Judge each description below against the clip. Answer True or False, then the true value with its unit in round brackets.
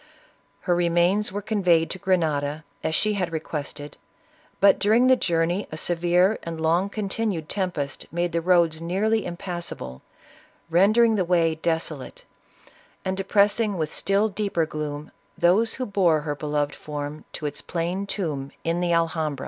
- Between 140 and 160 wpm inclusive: True (150 wpm)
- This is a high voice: False (175 Hz)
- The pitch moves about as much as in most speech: True (3.8 semitones)